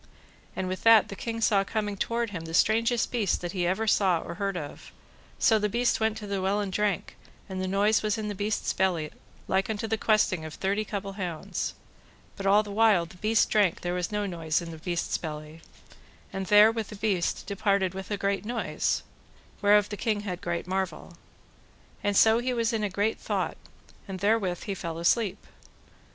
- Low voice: No, high, 200 Hz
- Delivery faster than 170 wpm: Yes, average, 200 wpm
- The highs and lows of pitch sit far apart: No, average, 2.7 semitones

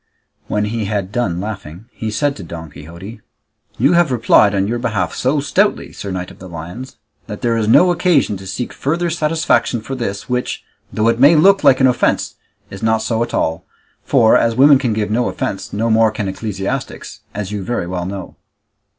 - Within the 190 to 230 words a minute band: Yes, average, 200 wpm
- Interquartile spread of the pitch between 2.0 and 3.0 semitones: No, average, 4.7 semitones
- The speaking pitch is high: No, low, 110 Hz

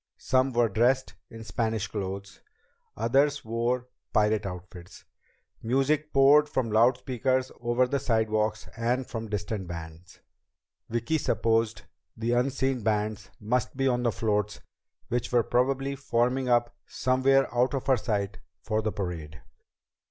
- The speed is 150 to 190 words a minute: No, slow, 135 wpm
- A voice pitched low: Yes, low, 120 Hz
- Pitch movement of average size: Yes, average, 3.3 semitones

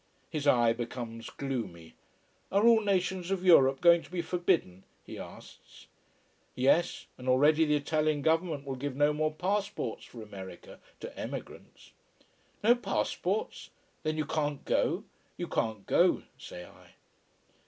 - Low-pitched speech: No, medium, 150 Hz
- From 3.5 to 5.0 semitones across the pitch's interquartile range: No, wide, 5.6 semitones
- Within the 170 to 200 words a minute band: No, average, 140 wpm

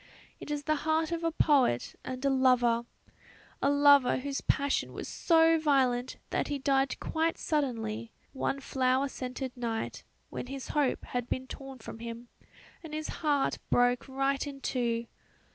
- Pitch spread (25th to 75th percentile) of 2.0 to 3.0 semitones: Yes, average, 2.7 semitones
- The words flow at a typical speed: Yes, average, 160 wpm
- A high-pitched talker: Yes, very high, 270 Hz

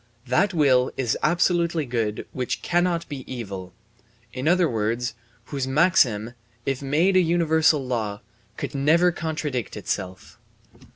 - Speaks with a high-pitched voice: No, medium, 140 Hz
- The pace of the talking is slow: Yes, slow, 125 wpm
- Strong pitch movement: Yes, wide, 5.8 semitones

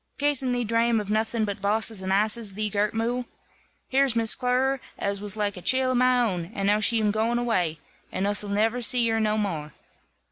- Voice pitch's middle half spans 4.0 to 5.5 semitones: No, average, 3.0 semitones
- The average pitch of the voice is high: Yes, high, 220 Hz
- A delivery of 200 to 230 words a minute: Yes, fast, 205 wpm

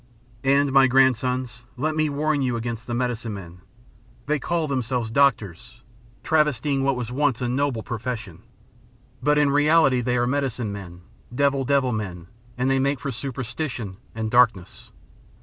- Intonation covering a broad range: No, average, 3.3 semitones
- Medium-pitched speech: No, low, 125 Hz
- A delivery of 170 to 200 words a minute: No, average, 150 wpm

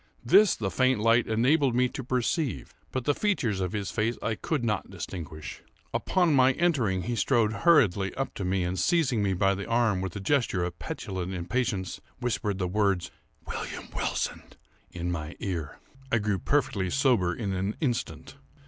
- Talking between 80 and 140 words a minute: No, average, 175 wpm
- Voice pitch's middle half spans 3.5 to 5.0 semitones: No, wide, 5.5 semitones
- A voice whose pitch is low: Yes, low, 105 Hz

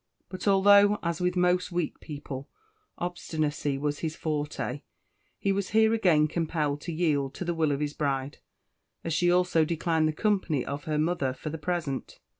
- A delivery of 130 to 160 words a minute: No, average, 175 wpm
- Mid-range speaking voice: Yes, medium, 160 Hz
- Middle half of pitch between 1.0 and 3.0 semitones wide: No, average, 3.4 semitones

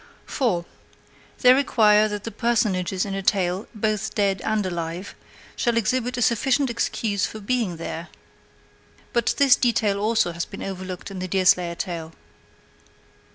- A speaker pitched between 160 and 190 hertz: No, high, 205 Hz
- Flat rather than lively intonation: No, average, 4.1 semitones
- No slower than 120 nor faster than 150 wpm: Yes, average, 145 wpm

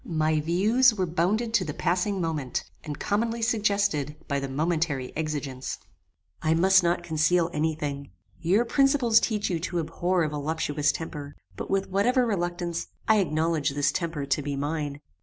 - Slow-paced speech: No, average, 160 wpm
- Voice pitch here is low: No, medium, 165 Hz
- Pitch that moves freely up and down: No, average, 4.8 semitones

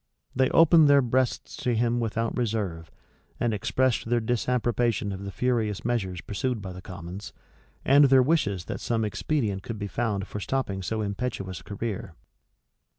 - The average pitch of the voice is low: Yes, low, 115 Hz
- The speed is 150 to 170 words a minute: Yes, average, 160 wpm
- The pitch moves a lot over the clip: No, average, 4.0 semitones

